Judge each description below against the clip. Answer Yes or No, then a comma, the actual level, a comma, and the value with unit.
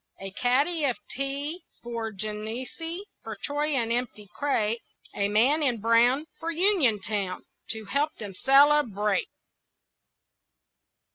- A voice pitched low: No, high, 245 Hz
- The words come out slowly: Yes, slow, 115 wpm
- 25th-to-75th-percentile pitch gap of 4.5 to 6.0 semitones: Yes, wide, 5.4 semitones